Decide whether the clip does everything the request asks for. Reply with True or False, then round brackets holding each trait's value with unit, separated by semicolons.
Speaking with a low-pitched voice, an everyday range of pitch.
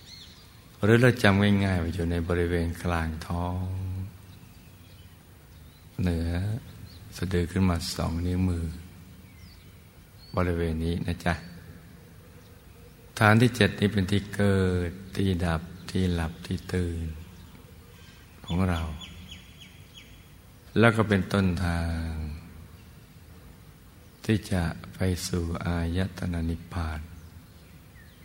False (90 Hz; 1.8 semitones)